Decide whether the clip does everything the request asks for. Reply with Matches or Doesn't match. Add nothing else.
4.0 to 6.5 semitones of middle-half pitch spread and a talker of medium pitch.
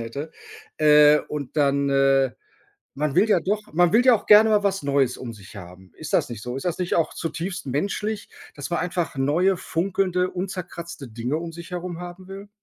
Matches